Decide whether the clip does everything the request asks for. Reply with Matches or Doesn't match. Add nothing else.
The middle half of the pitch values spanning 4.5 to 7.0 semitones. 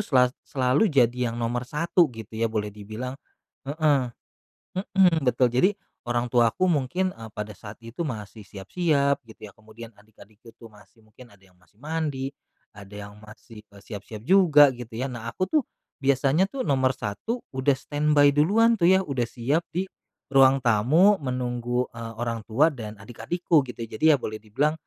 Matches